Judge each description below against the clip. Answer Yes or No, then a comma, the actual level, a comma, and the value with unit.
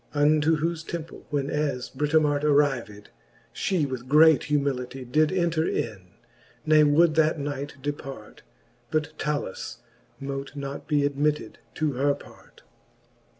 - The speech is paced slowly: Yes, slow, 130 wpm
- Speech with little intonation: Yes, narrow, 2.1 semitones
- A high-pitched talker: No, medium, 145 Hz